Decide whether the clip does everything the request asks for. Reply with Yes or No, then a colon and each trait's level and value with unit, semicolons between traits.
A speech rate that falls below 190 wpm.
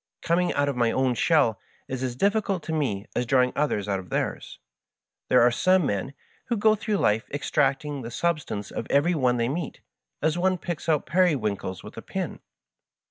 No: average, 195 wpm